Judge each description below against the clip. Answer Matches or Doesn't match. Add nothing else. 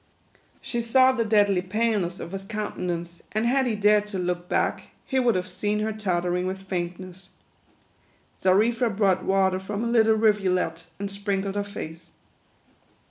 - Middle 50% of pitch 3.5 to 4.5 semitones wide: Doesn't match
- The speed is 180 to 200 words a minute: Doesn't match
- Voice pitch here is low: Doesn't match